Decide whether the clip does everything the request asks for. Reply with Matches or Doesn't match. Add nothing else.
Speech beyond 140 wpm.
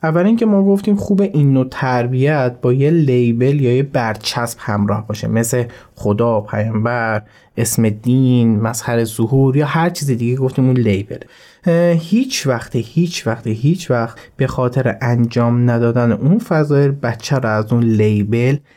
Matches